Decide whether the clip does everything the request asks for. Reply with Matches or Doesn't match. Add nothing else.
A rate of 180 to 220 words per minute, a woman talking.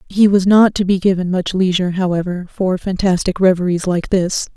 Matches